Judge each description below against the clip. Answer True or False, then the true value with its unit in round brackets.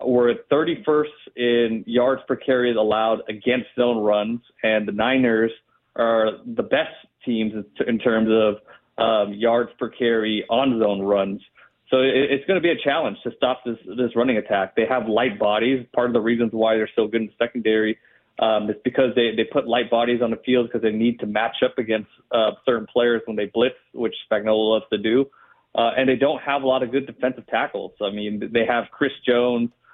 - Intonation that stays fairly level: True (2.3 semitones)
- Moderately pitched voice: False (120 Hz)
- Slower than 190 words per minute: False (200 wpm)